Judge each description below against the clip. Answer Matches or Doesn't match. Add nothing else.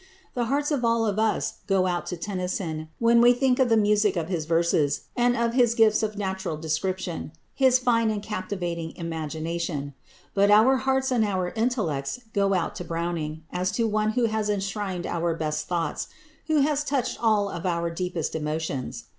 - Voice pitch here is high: Matches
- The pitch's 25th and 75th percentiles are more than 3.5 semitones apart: Matches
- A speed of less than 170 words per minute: Doesn't match